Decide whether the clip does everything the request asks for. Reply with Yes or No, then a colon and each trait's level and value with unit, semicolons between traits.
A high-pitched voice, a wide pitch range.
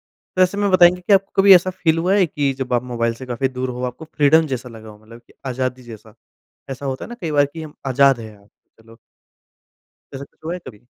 No: low, 135 Hz; wide, 5.7 semitones